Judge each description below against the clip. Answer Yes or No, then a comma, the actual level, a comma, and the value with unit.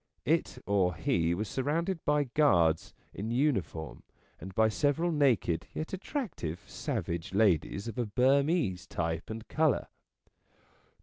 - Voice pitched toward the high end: No, low, 110 Hz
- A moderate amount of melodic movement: No, wide, 8.9 semitones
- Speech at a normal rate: No, slow, 125 wpm